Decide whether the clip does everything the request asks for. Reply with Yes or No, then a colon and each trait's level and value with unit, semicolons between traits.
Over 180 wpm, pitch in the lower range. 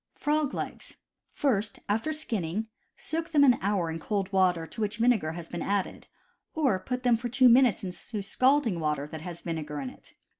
No: average, 190 wpm; high, 210 Hz